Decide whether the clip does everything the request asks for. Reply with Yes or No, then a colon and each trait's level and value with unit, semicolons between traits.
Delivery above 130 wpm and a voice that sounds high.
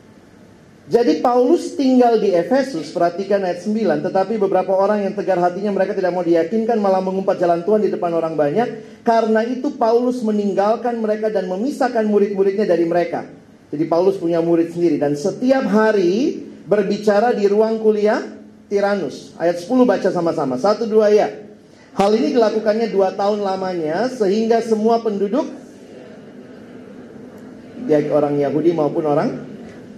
Yes: fast, 140 wpm; high, 205 Hz